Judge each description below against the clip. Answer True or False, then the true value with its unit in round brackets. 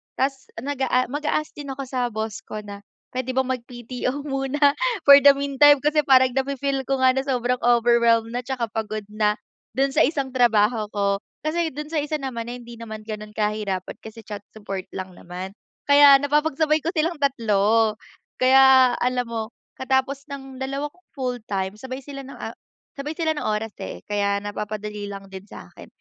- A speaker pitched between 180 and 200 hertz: False (255 Hz)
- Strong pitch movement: False (4.4 semitones)